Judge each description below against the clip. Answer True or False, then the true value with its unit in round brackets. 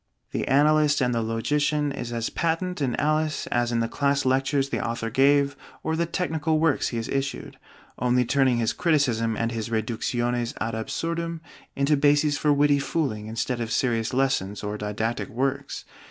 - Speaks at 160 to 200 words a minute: True (170 wpm)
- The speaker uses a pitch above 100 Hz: True (135 Hz)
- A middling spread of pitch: True (4.1 semitones)